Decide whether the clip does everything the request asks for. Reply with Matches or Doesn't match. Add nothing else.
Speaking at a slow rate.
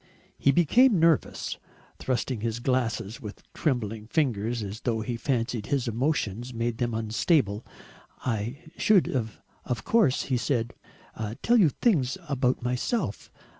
Matches